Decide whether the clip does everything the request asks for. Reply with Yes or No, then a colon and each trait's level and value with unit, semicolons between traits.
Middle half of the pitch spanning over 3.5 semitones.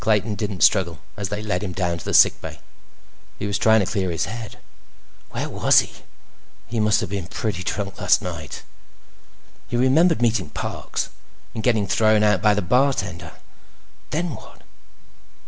No: average, 3.0 semitones